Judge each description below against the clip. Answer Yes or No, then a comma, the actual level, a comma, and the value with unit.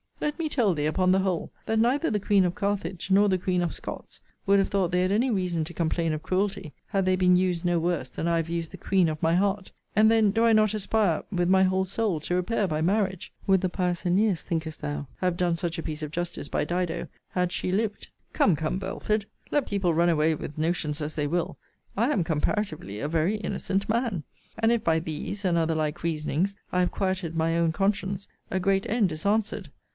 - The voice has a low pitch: No, medium, 180 Hz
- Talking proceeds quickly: Yes, fast, 230 wpm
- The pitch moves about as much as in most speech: Yes, average, 3.3 semitones